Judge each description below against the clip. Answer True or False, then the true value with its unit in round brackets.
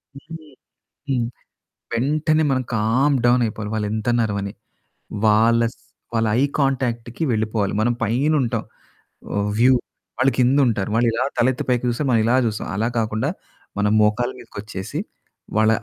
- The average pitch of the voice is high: False (115 Hz)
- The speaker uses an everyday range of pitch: True (3.0 semitones)